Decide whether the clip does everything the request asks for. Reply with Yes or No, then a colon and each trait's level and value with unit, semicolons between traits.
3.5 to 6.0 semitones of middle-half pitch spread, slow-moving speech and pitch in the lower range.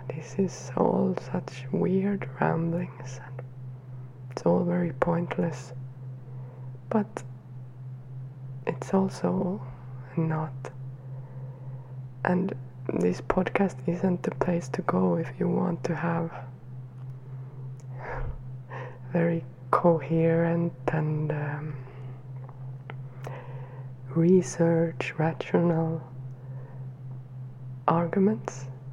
Yes: average, 4.3 semitones; slow, 75 wpm; low, 130 Hz